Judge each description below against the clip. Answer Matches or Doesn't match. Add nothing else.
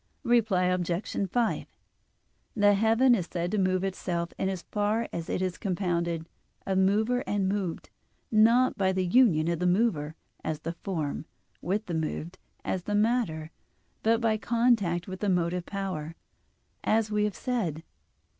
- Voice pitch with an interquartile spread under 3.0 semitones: Doesn't match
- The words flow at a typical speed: Matches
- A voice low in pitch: Doesn't match